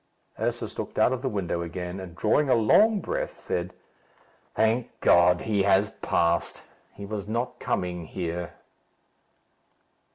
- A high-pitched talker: No, very low, 95 Hz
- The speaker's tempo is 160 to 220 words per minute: No, slow, 135 wpm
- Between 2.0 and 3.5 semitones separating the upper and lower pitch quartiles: No, average, 4.2 semitones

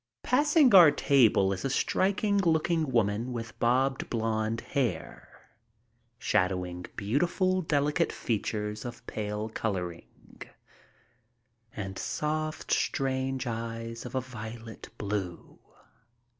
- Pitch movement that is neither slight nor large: No, wide, 5.8 semitones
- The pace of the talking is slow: Yes, slow, 100 wpm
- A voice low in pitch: Yes, low, 120 Hz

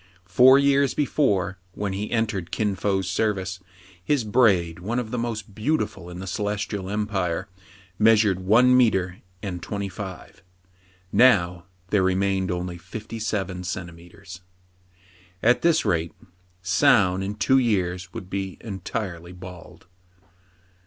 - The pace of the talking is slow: Yes, slow, 130 wpm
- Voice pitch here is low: Yes, low, 100 Hz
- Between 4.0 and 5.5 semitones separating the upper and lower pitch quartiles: No, average, 3.4 semitones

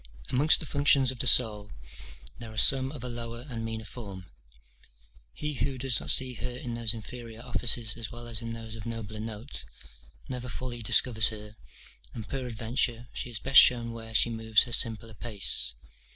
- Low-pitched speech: Yes, low, 115 Hz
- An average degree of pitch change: No, narrow, 2.1 semitones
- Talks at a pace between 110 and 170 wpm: No, average, 180 wpm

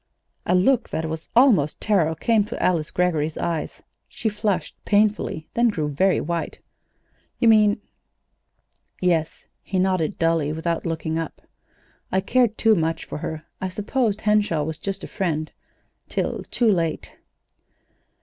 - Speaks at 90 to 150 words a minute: Yes, average, 145 wpm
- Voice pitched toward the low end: No, medium, 180 Hz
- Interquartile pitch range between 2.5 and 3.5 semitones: No, average, 4.7 semitones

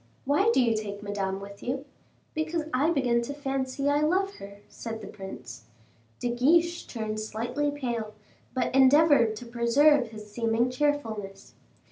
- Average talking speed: Yes, average, 150 wpm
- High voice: Yes, high, 245 Hz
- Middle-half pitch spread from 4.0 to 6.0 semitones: Yes, average, 5.1 semitones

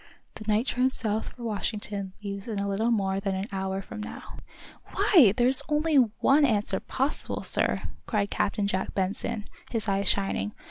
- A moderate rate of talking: Yes, average, 170 wpm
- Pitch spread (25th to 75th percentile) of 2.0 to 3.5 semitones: Yes, average, 3.1 semitones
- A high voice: Yes, high, 210 Hz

